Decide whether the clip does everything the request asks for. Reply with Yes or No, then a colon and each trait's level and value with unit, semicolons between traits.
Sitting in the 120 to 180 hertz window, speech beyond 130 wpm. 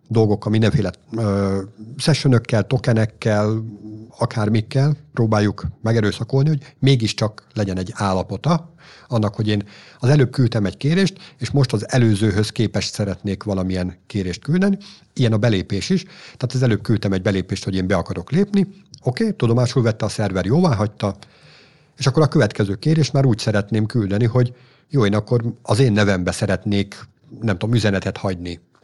No: low, 110 Hz; fast, 155 wpm